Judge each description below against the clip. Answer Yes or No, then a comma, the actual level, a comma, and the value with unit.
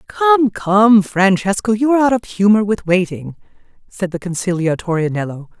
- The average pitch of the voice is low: No, high, 200 Hz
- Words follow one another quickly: No, average, 150 wpm